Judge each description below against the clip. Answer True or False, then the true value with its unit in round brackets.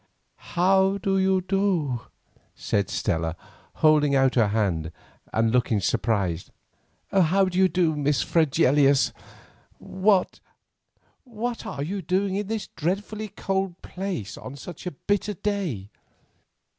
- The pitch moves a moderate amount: False (7.4 semitones)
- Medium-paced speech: False (120 wpm)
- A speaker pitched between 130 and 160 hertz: False (175 Hz)